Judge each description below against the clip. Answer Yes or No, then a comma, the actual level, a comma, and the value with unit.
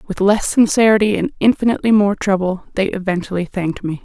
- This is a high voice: Yes, high, 200 Hz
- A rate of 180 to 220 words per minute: No, average, 165 wpm